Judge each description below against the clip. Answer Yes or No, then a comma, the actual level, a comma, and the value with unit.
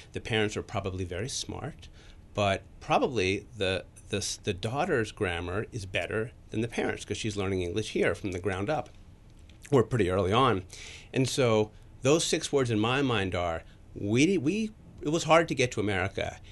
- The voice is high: No, low, 105 Hz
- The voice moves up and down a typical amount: Yes, average, 3.9 semitones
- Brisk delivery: No, average, 180 wpm